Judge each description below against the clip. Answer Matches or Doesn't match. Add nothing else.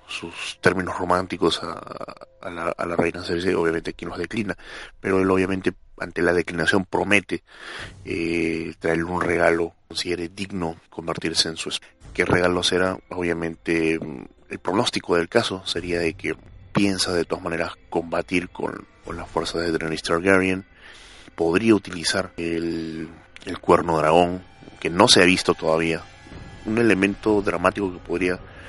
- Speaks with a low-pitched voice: Matches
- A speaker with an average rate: Matches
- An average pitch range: Doesn't match